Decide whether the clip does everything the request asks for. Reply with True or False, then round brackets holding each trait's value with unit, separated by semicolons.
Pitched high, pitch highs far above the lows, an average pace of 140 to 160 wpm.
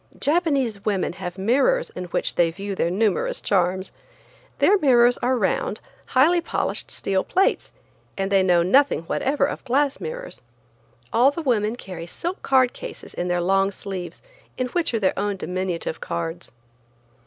True (210 Hz; 6.8 semitones; 155 wpm)